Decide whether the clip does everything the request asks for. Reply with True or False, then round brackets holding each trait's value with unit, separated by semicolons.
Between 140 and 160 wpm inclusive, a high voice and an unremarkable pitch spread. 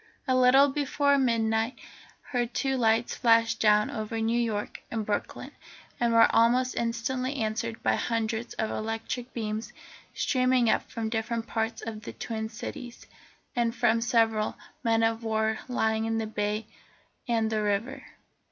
False (150 wpm; 230 Hz; 1.6 semitones)